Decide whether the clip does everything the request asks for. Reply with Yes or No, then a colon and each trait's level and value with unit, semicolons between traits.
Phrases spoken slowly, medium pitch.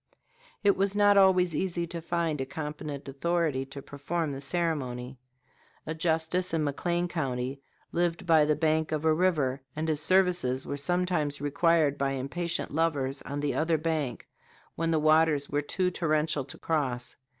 No: average, 160 wpm; medium, 155 Hz